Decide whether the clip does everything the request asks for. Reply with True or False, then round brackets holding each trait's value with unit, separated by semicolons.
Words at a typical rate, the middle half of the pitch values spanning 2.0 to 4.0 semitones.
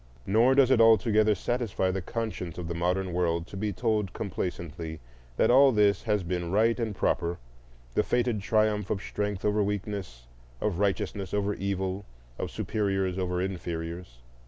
True (160 wpm; 3.1 semitones)